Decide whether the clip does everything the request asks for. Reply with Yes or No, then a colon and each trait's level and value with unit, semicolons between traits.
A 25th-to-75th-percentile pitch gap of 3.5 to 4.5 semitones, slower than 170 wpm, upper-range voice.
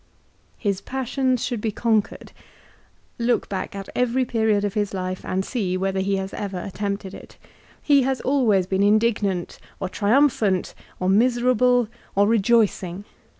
Yes: average, 3.9 semitones; average, 145 wpm; high, 210 Hz